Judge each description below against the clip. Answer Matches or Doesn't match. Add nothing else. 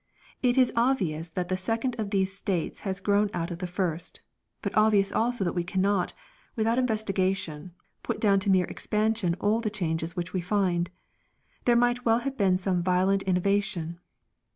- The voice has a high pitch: Matches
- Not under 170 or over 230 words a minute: Matches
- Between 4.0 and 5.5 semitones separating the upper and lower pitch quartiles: Doesn't match